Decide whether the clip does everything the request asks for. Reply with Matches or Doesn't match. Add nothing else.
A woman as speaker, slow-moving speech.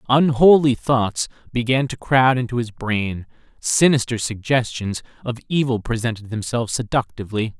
Doesn't match